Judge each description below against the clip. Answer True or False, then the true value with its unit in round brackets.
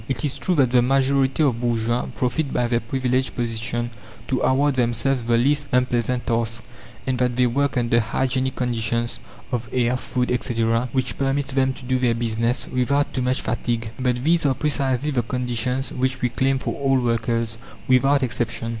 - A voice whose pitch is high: False (125 Hz)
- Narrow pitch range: True (2.1 semitones)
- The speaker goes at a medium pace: True (180 wpm)